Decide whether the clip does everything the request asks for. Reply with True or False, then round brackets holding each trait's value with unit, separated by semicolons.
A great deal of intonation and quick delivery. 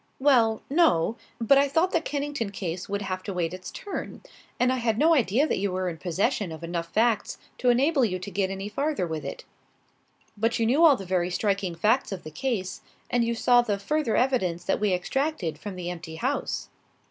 True (6.5 semitones; 210 wpm)